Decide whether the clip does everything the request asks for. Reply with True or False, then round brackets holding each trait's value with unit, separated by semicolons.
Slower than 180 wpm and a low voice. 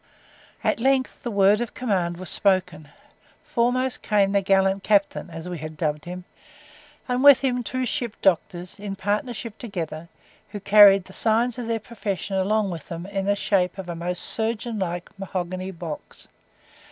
False (165 wpm; 195 Hz)